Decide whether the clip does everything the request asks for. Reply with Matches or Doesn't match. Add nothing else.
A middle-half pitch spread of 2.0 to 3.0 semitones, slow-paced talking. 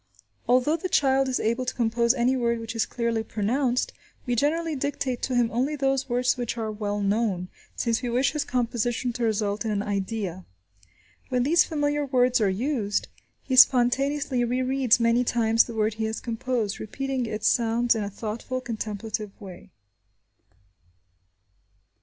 Doesn't match